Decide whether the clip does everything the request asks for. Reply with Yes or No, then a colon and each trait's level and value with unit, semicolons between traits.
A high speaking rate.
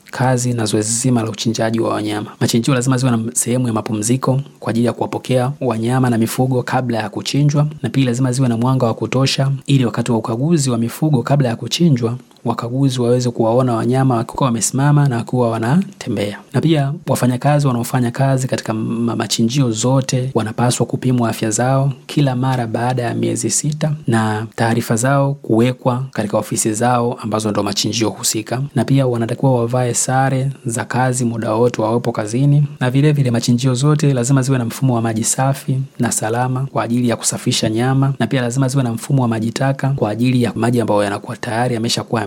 Yes: fast, 180 wpm